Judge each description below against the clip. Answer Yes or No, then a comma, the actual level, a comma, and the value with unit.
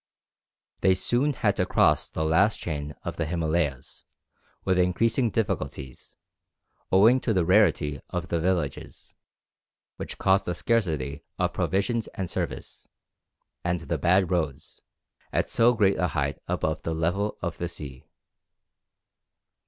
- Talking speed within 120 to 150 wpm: Yes, slow, 135 wpm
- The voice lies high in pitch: No, very low, 90 Hz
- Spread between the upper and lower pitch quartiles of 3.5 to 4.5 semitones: Yes, average, 4.1 semitones